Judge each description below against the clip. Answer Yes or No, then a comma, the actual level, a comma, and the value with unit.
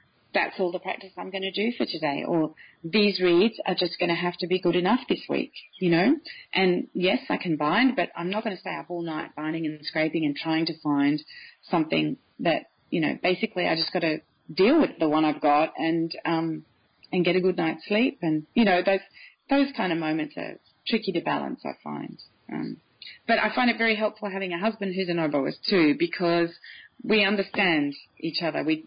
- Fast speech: Yes, fast, 210 wpm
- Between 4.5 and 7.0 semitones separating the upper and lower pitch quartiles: No, average, 3.8 semitones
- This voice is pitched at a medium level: Yes, medium, 175 Hz